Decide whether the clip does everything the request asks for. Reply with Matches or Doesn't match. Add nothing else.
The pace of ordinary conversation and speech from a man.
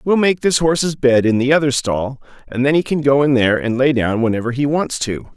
Doesn't match